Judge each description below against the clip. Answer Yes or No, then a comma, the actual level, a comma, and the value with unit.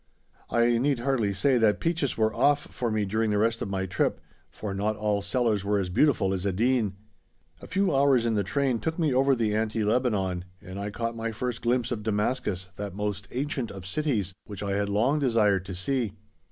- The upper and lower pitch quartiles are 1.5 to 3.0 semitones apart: No, average, 3.9 semitones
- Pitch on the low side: Yes, low, 110 Hz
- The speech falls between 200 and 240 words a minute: Yes, fast, 205 wpm